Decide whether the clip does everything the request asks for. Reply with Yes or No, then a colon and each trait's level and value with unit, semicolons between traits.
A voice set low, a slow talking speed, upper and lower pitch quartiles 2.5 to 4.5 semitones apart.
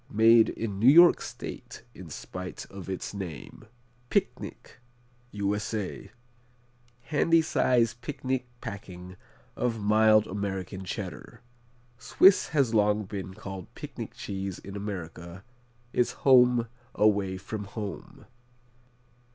Yes: low, 105 Hz; slow, 105 wpm; average, 3.5 semitones